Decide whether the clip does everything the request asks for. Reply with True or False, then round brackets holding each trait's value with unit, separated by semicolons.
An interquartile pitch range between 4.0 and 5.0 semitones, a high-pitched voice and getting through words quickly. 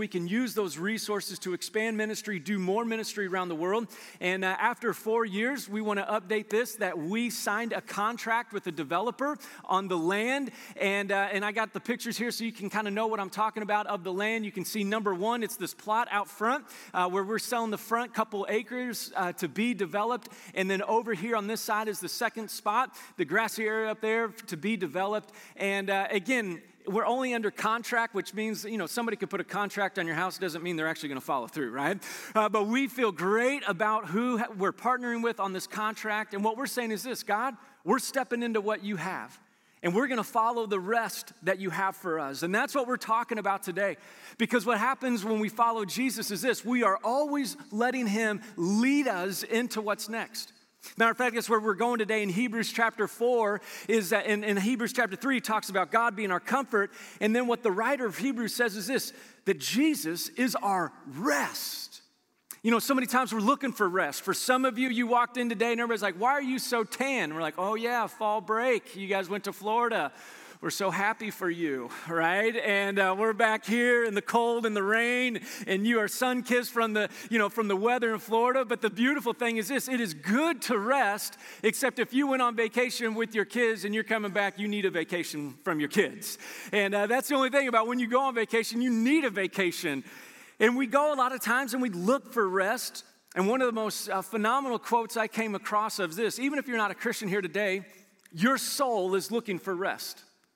False (3.1 semitones; 220 Hz; 230 wpm)